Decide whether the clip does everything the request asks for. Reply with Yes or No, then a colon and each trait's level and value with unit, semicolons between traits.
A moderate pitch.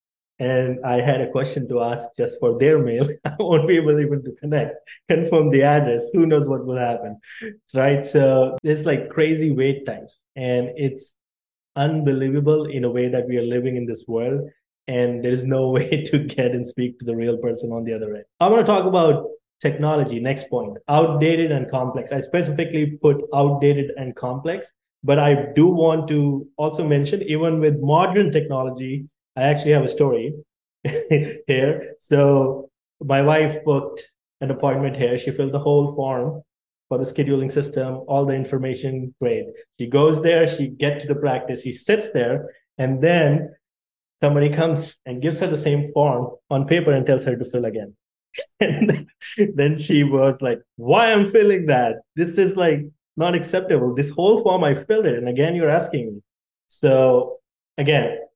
Yes: medium, 145 Hz